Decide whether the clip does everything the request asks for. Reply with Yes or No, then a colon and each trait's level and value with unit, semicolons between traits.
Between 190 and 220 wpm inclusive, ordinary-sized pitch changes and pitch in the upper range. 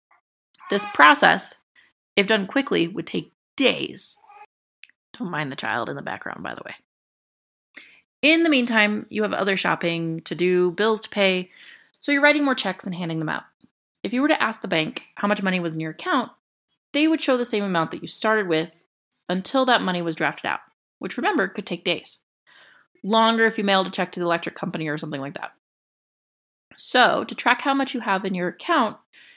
No: average, 200 wpm; wide, 6.1 semitones; high, 200 Hz